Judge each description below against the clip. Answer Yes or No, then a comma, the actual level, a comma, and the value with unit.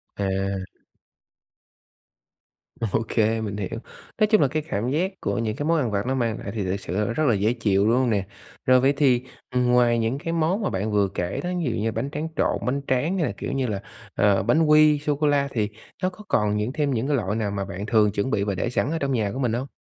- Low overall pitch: Yes, low, 120 Hz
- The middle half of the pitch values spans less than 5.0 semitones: No, wide, 5.6 semitones